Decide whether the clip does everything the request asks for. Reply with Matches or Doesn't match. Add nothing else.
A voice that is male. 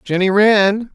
Matches